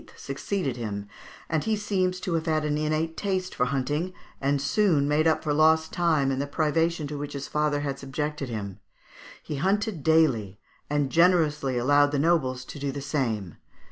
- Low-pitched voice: No, medium, 150 Hz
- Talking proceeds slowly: No, average, 180 wpm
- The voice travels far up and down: No, average, 3.1 semitones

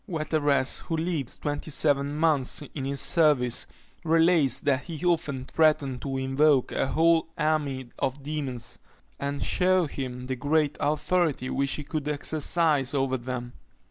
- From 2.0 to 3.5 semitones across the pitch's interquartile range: Yes, average, 2.9 semitones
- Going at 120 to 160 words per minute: Yes, average, 140 wpm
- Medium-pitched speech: Yes, medium, 145 Hz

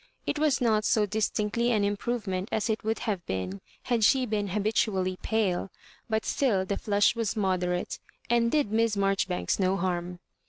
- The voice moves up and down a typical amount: Yes, average, 3.1 semitones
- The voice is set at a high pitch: Yes, high, 210 Hz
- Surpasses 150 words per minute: Yes, average, 170 wpm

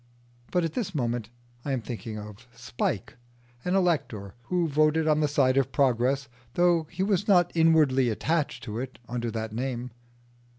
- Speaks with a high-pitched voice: No, low, 135 Hz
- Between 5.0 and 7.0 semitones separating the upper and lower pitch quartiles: Yes, wide, 5.4 semitones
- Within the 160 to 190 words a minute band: Yes, average, 165 wpm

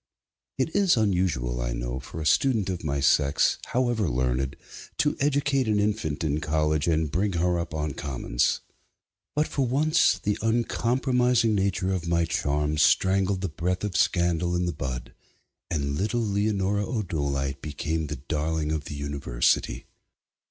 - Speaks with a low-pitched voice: Yes, very low, 85 Hz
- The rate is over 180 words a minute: No, average, 150 wpm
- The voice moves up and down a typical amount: No, wide, 6.2 semitones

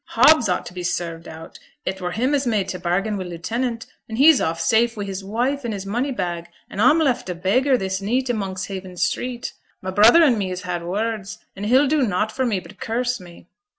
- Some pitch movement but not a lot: Yes, average, 5.0 semitones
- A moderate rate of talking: No, fast, 225 wpm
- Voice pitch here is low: No, high, 205 Hz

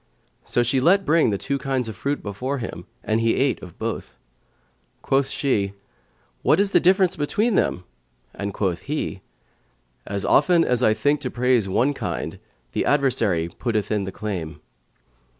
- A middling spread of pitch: No, wide, 5.9 semitones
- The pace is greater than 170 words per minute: No, average, 165 wpm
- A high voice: No, low, 125 Hz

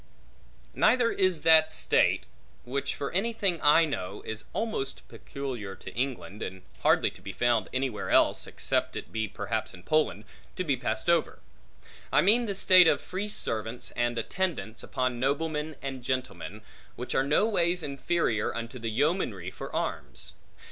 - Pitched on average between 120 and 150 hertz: Yes, low, 135 Hz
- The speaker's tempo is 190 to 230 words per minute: No, average, 160 wpm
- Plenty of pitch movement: Yes, wide, 7.1 semitones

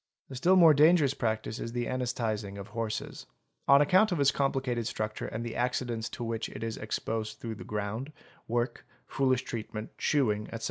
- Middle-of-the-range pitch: No, low, 120 Hz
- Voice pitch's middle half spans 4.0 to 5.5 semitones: No, average, 3.6 semitones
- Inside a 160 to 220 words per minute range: Yes, average, 185 wpm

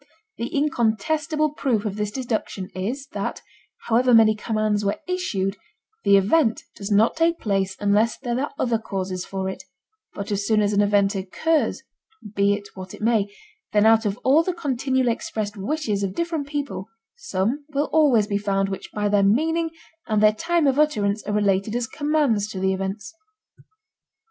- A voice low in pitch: No, high, 215 Hz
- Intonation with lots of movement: Yes, wide, 6.0 semitones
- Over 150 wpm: Yes, average, 170 wpm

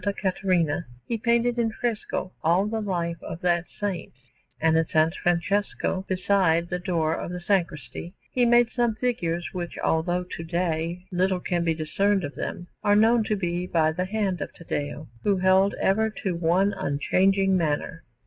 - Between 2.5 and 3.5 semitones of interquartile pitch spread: Yes, average, 3.2 semitones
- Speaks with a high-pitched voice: No, medium, 180 Hz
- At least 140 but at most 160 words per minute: No, average, 170 wpm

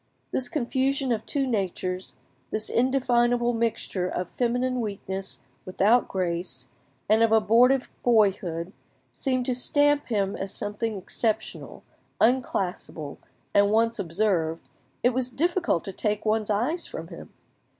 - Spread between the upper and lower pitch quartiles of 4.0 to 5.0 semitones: Yes, average, 4.4 semitones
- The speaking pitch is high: Yes, high, 220 Hz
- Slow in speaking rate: Yes, slow, 125 wpm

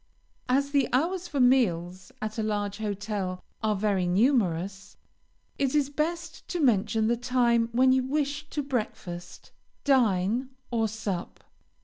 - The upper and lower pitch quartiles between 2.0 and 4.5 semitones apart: No, average, 5.3 semitones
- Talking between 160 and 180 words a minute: No, slow, 135 wpm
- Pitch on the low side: No, high, 230 Hz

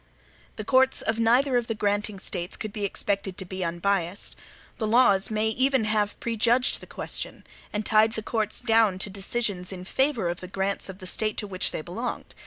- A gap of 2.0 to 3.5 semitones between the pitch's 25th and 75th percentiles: Yes, average, 3.0 semitones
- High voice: Yes, high, 210 Hz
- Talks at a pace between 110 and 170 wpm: No, average, 195 wpm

